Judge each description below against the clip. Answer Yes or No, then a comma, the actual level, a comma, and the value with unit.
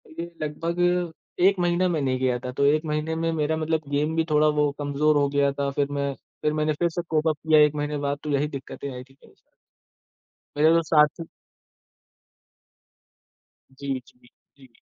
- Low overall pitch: No, medium, 150 Hz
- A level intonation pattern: Yes, narrow, 2.2 semitones